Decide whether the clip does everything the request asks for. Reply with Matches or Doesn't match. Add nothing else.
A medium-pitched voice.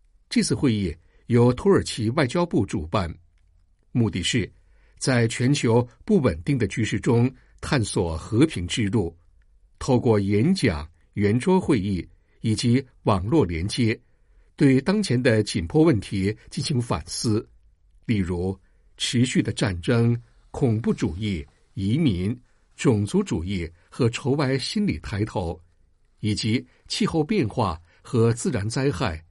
Doesn't match